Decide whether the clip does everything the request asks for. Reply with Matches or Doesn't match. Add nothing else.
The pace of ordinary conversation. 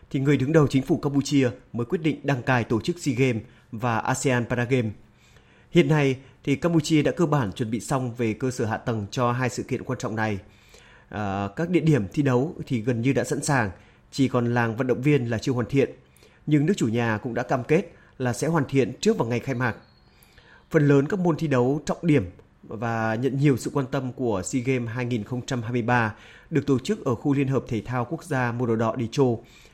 Matches